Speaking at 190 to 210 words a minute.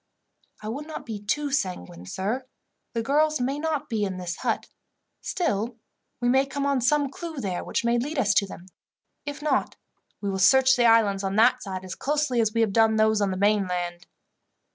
Yes: average, 200 wpm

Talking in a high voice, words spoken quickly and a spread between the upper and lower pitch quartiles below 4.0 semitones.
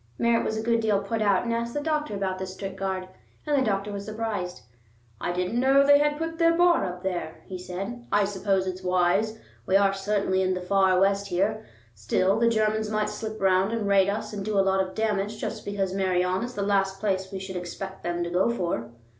Yes: high, 200 Hz; fast, 230 wpm; average, 2.7 semitones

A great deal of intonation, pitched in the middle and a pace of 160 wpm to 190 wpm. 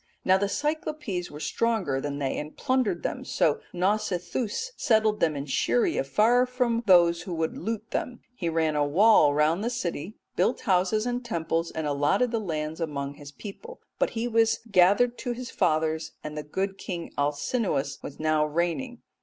Yes: wide, 6.9 semitones; medium, 180 Hz; average, 180 wpm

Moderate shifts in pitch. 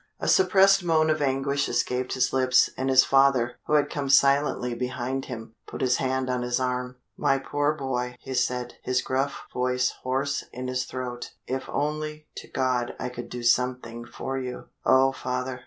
No: narrow, 1.6 semitones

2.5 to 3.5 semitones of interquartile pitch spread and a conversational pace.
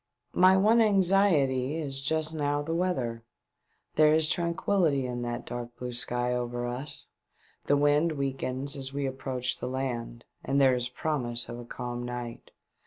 No: average, 4.1 semitones; average, 160 wpm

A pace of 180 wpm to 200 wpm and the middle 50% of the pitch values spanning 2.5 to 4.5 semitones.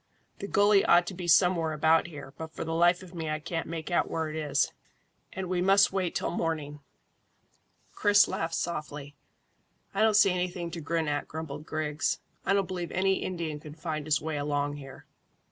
Yes: average, 195 wpm; average, 3.0 semitones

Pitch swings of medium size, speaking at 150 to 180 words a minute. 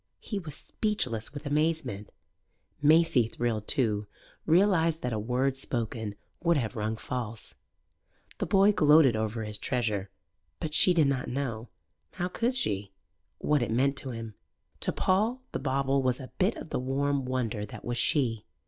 No: wide, 5.8 semitones; average, 160 wpm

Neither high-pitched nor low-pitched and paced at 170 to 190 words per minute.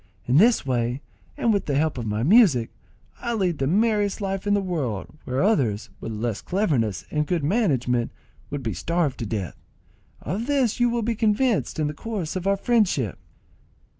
Yes: medium, 170 Hz; average, 185 wpm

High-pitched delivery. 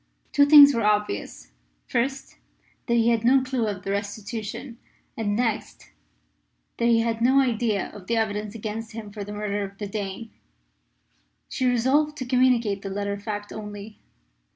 Yes: high, 220 Hz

